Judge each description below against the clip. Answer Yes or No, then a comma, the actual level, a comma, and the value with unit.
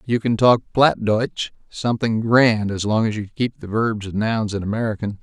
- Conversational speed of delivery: Yes, average, 195 wpm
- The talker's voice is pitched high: No, low, 110 Hz